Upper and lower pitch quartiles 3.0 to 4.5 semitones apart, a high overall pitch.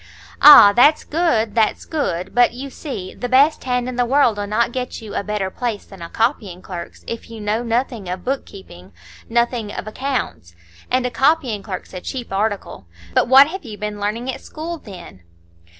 Yes: average, 4.1 semitones; high, 230 Hz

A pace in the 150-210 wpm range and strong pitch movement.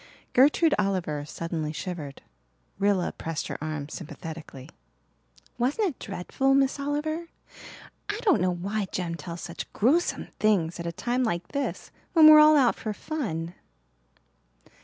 No: average, 140 wpm; wide, 9.0 semitones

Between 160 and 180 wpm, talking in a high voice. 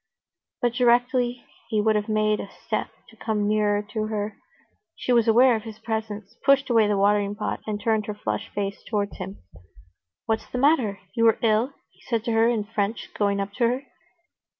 No: average, 195 wpm; high, 220 Hz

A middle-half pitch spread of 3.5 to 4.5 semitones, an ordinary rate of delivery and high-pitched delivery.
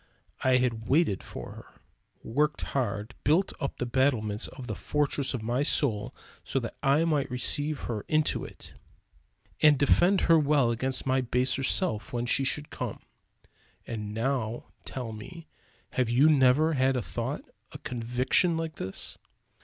No: average, 3.8 semitones; average, 155 wpm; low, 130 Hz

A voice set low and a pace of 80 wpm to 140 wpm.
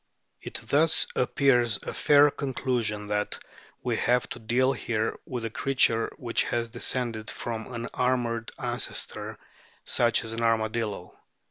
Yes: low, 120 Hz; slow, 135 wpm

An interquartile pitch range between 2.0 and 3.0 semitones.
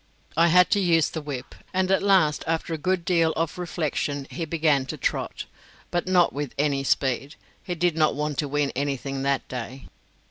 No: average, 3.6 semitones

